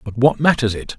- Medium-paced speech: No, fast, 245 wpm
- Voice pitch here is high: No, low, 120 Hz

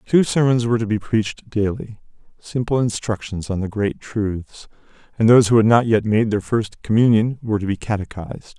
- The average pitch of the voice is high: No, low, 110 Hz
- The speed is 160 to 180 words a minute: Yes, average, 175 wpm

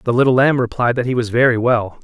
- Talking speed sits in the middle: No, fast, 265 wpm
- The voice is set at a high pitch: No, low, 120 Hz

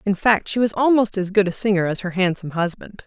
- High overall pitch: Yes, high, 200 Hz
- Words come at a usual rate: No, fast, 255 wpm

